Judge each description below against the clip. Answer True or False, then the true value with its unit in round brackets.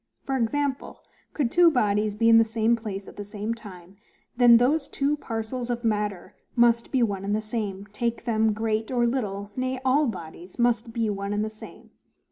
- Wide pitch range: False (2.7 semitones)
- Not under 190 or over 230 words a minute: True (195 wpm)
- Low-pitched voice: False (225 Hz)